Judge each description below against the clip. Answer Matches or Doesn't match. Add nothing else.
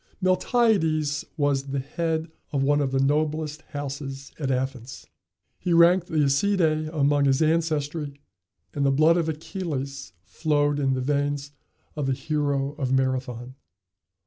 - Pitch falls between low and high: Matches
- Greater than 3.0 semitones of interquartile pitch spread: Doesn't match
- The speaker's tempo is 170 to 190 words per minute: Doesn't match